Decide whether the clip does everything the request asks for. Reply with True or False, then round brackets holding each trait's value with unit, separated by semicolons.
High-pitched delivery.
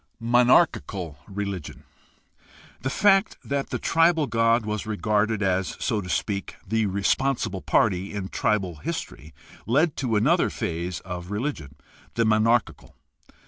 False (105 Hz)